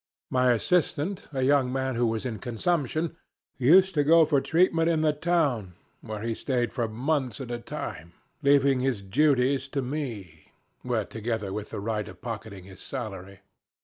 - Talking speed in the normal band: Yes, average, 165 wpm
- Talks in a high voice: No, low, 130 Hz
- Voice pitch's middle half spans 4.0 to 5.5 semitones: Yes, average, 5.1 semitones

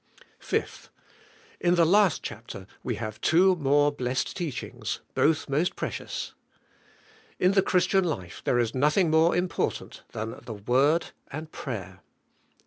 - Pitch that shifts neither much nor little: No, wide, 6.1 semitones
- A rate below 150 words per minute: Yes, slow, 135 wpm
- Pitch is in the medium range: Yes, medium, 150 Hz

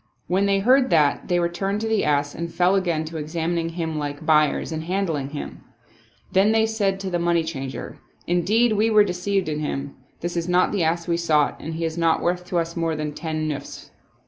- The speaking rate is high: Yes, fast, 225 wpm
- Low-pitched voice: No, medium, 170 Hz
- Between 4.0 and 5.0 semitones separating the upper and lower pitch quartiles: No, average, 3.5 semitones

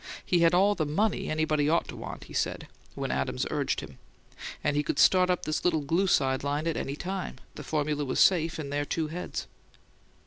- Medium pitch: Yes, medium, 155 Hz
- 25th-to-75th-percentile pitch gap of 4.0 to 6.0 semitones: No, average, 3.5 semitones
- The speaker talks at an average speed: No, fast, 210 wpm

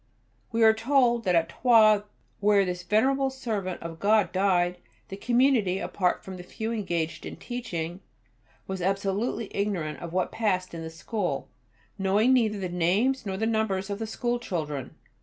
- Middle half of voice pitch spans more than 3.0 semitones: Yes, average, 4.0 semitones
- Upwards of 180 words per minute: No, average, 165 wpm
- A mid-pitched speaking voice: No, high, 200 Hz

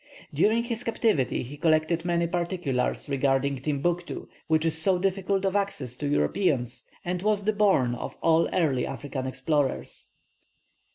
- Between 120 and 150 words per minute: Yes, average, 145 wpm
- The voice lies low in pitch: No, medium, 160 Hz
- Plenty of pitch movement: Yes, wide, 5.7 semitones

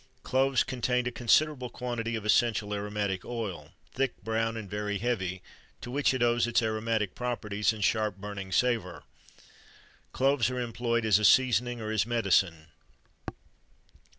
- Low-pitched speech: Yes, low, 115 Hz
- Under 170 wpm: Yes, average, 145 wpm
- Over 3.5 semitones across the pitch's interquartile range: No, average, 2.9 semitones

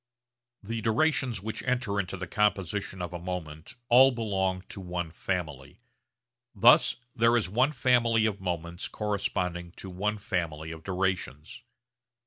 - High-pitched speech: No, very low, 95 Hz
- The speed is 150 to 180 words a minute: No, slow, 135 wpm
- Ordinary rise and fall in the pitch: Yes, average, 4.1 semitones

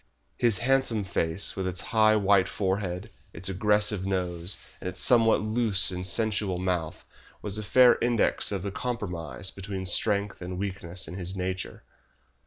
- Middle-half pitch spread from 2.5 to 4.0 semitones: Yes, average, 2.8 semitones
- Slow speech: No, average, 155 wpm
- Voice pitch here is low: Yes, very low, 95 Hz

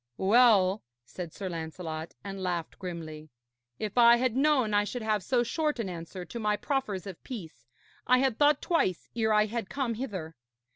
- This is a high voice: Yes, high, 210 Hz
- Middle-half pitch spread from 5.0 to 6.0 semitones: Yes, average, 5.3 semitones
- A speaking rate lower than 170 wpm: No, average, 180 wpm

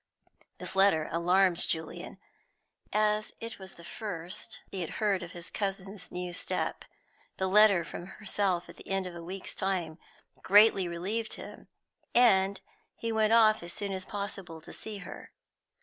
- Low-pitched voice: No, high, 190 Hz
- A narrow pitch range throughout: No, average, 3.2 semitones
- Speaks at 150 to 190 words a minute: Yes, average, 160 wpm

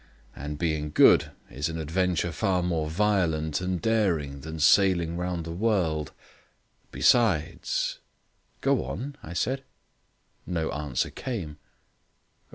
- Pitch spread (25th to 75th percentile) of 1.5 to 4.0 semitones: Yes, average, 3.4 semitones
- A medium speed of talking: No, slow, 120 wpm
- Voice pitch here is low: Yes, very low, 85 Hz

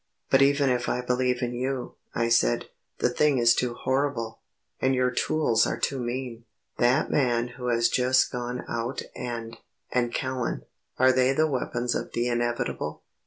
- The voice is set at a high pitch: No, low, 125 Hz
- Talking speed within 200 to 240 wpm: No, average, 165 wpm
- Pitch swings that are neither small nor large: No, narrow, 1.5 semitones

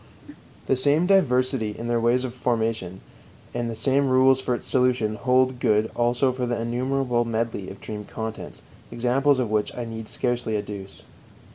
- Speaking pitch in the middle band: No, low, 120 Hz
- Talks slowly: No, average, 165 wpm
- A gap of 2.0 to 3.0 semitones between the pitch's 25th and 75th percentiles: Yes, narrow, 2.6 semitones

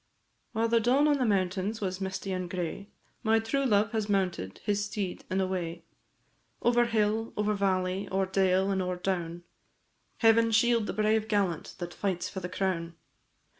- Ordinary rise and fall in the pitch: Yes, average, 3.1 semitones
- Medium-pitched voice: No, high, 195 Hz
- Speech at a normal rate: Yes, average, 170 wpm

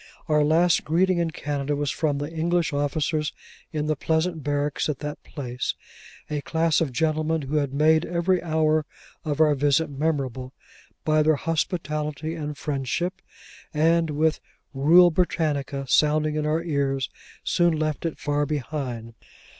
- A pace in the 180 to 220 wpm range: No, average, 145 wpm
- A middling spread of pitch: No, narrow, 1.9 semitones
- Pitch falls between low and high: Yes, medium, 155 Hz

